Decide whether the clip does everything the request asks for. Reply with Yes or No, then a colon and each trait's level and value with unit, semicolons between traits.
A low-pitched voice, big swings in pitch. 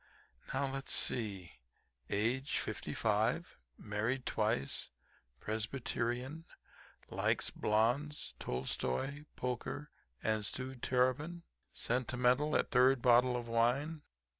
No: low, 125 Hz; average, 3.2 semitones